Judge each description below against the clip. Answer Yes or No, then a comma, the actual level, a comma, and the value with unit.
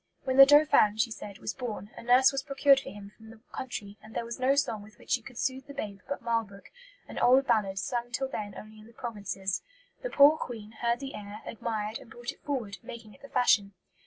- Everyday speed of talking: No, fast, 235 wpm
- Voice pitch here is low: No, high, 230 Hz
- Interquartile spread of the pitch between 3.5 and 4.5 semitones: Yes, average, 4.0 semitones